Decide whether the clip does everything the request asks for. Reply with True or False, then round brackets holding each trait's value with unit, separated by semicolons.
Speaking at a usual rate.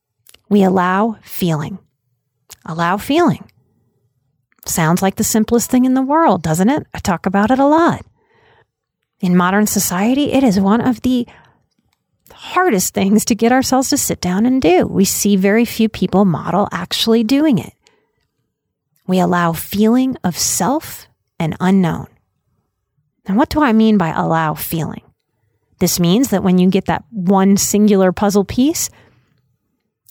True (145 wpm)